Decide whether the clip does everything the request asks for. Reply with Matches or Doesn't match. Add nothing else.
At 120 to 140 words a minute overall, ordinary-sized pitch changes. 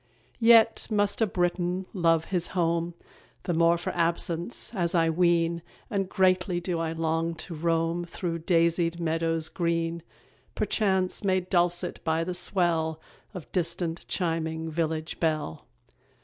Doesn't match